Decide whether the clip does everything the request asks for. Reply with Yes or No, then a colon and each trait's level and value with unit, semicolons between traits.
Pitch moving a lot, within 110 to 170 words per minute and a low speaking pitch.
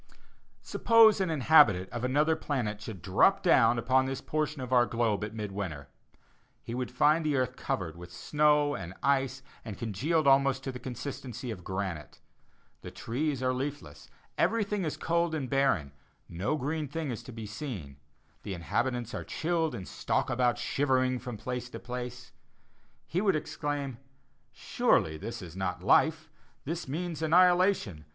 Yes: wide, 6.0 semitones; average, 160 wpm; low, 130 Hz